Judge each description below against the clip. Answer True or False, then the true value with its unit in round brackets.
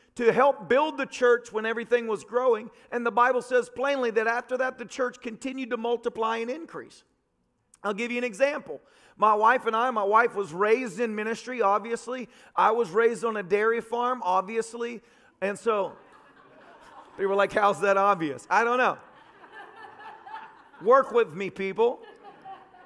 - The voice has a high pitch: True (235 Hz)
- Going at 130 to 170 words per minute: True (165 wpm)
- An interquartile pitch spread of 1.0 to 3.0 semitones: True (2.5 semitones)